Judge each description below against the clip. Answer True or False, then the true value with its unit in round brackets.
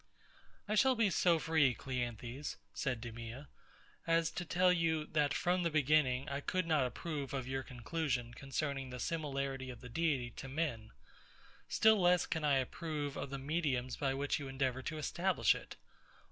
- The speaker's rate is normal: True (170 wpm)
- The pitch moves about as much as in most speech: True (4.0 semitones)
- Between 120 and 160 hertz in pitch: True (140 Hz)